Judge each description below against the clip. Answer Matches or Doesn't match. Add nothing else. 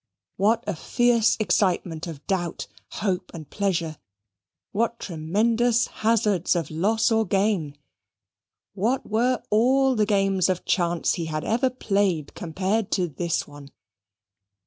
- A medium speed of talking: Doesn't match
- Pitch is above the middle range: Matches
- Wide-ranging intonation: Doesn't match